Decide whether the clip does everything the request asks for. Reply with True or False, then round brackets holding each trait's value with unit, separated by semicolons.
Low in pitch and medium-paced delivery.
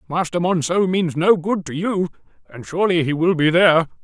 False (170 Hz; 195 wpm)